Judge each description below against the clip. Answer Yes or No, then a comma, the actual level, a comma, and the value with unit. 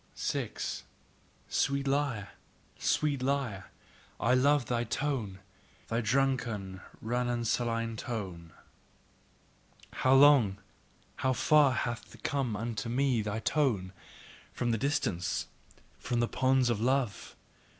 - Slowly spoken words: Yes, slow, 105 wpm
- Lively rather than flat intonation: No, average, 3.7 semitones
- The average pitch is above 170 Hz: No, low, 120 Hz